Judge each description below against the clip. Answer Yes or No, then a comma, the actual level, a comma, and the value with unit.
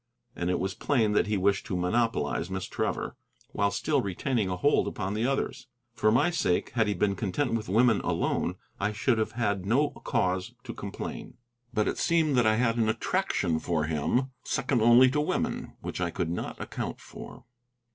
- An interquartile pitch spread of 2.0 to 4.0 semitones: No, average, 4.7 semitones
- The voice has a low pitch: Yes, low, 110 Hz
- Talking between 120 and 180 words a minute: No, average, 190 wpm